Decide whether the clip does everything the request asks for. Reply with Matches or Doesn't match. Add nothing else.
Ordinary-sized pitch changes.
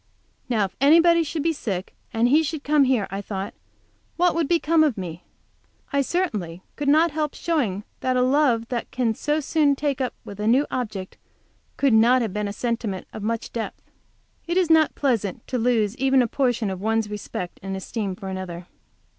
Doesn't match